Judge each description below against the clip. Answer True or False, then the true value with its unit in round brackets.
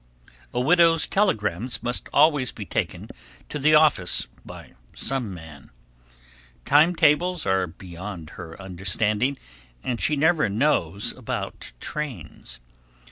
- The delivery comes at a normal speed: False (115 wpm)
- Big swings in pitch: True (8.5 semitones)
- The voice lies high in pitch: False (120 Hz)